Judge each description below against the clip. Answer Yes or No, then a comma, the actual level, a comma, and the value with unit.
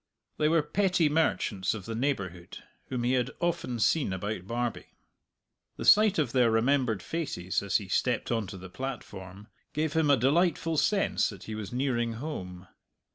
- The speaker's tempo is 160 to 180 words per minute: Yes, average, 170 wpm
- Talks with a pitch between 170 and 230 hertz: No, low, 120 Hz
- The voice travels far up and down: Yes, wide, 6.7 semitones